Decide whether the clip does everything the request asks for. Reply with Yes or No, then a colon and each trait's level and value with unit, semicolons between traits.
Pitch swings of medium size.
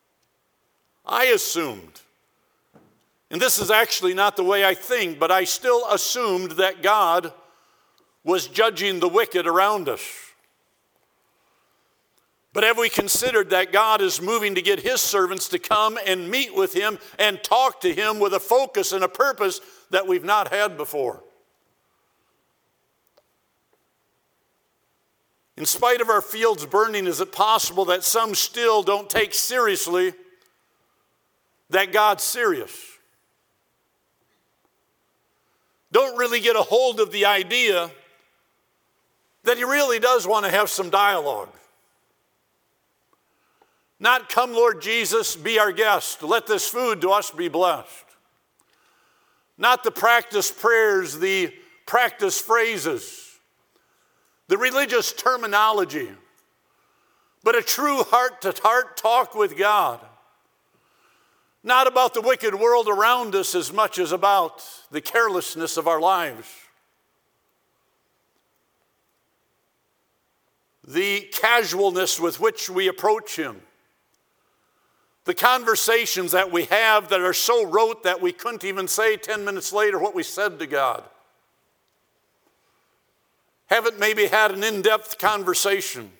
Yes: average, 4.9 semitones